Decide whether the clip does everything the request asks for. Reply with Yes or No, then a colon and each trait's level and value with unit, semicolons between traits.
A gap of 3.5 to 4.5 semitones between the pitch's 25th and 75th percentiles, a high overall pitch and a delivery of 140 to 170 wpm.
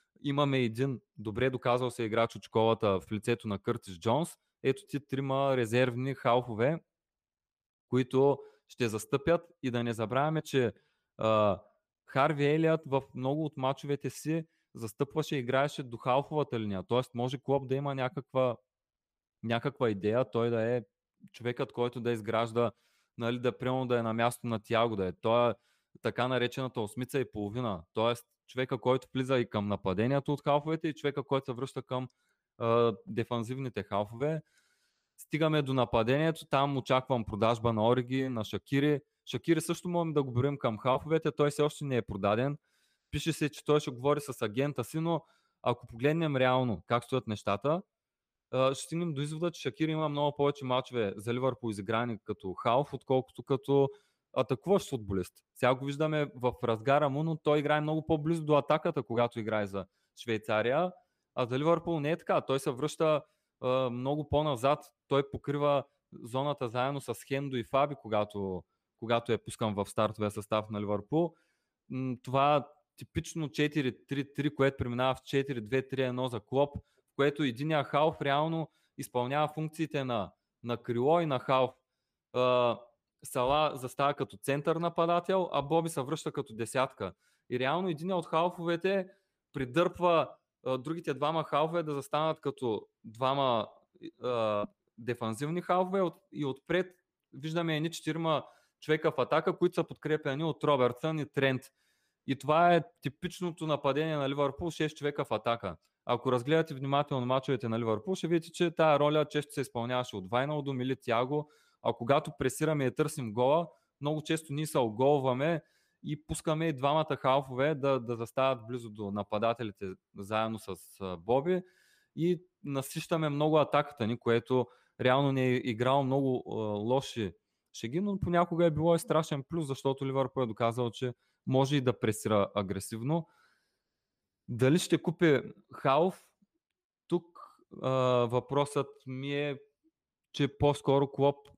No: average, 4.1 semitones; low, 135 Hz; average, 150 wpm